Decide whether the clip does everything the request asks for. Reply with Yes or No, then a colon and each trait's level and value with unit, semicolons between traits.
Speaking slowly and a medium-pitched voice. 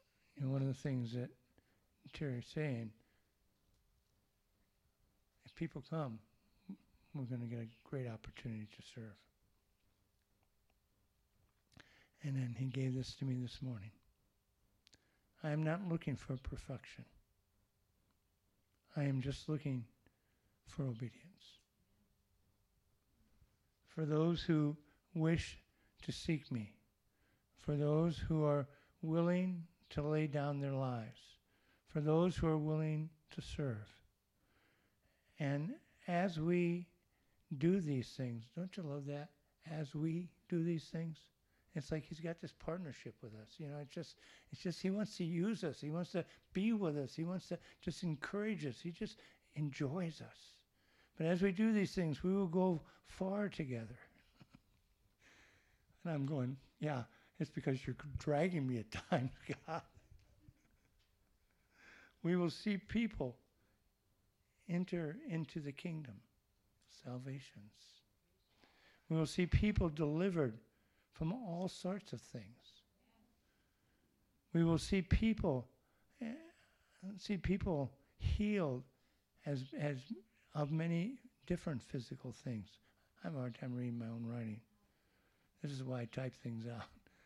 Yes: slow, 130 wpm; medium, 145 Hz